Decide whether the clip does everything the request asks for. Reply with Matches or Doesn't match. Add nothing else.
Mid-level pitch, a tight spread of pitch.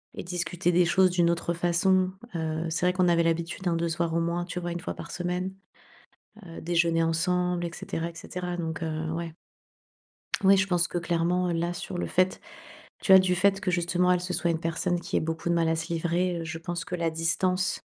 Matches